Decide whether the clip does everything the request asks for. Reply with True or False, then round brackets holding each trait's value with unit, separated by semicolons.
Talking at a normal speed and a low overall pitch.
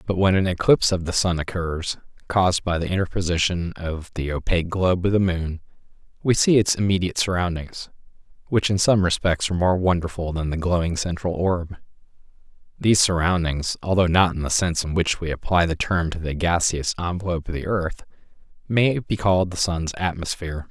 True (180 wpm; 90 Hz)